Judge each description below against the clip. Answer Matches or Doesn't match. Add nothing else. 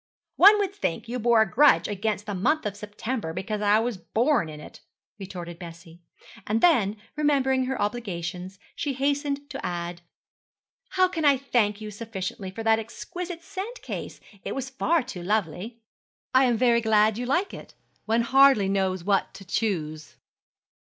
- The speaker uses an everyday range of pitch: Doesn't match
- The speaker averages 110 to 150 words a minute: Doesn't match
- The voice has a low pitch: Doesn't match